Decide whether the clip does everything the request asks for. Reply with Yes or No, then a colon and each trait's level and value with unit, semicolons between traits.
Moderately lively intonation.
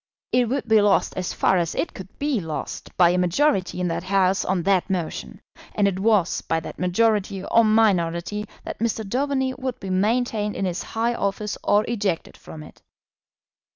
Yes: average, 3.8 semitones